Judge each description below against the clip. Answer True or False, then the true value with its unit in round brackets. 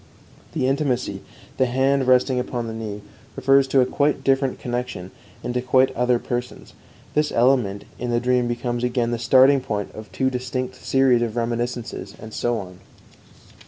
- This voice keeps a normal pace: True (165 wpm)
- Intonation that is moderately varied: False (1.8 semitones)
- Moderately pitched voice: False (125 Hz)